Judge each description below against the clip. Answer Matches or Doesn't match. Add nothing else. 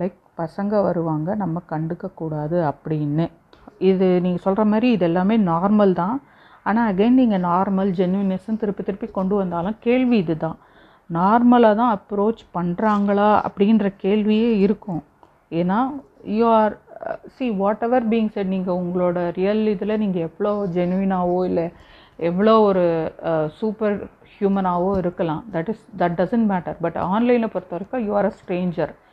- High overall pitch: Matches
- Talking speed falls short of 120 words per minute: Doesn't match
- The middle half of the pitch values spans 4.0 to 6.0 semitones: Doesn't match